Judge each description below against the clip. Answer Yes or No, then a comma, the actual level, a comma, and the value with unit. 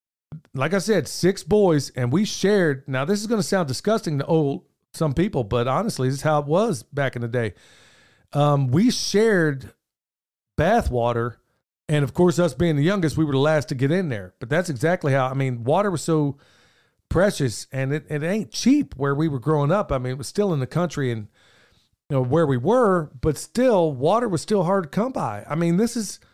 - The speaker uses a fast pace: Yes, fast, 220 wpm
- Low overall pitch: No, medium, 155 Hz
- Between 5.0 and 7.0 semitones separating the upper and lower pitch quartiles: Yes, wide, 5.6 semitones